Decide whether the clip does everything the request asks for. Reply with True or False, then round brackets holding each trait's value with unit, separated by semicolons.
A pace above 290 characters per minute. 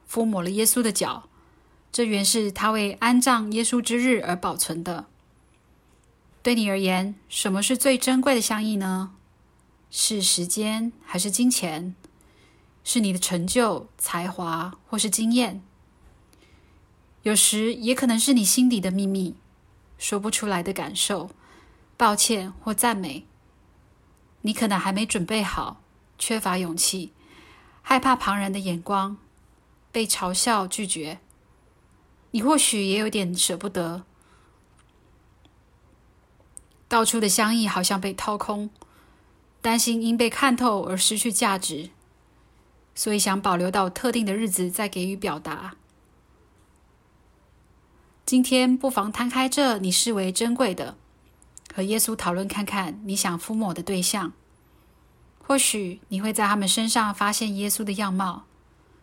False (195 characters per minute)